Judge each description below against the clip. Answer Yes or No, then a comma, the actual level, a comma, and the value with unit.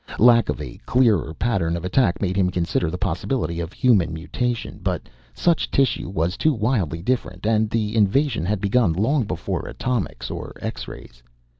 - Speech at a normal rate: Yes, average, 170 wpm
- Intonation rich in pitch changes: Yes, wide, 5.7 semitones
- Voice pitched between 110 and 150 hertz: No, low, 100 Hz